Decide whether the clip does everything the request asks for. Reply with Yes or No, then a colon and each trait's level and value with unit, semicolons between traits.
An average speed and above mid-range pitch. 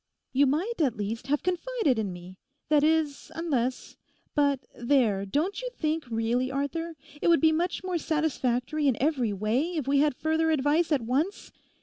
Yes: average, 165 wpm; very high, 290 Hz